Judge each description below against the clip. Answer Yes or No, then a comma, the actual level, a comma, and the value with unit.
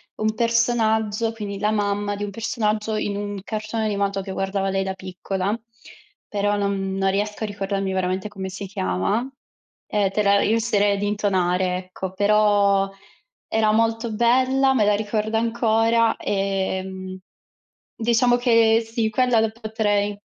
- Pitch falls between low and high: No, high, 205 Hz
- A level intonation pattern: Yes, narrow, 2.3 semitones